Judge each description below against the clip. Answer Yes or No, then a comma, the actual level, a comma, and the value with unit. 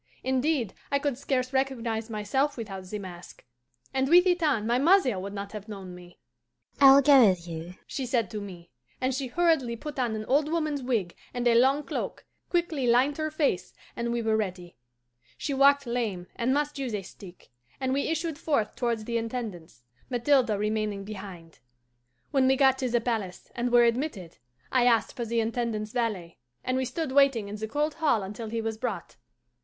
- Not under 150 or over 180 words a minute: No, average, 190 wpm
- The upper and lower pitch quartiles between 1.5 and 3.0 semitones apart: No, average, 4.5 semitones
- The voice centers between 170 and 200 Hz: No, high, 240 Hz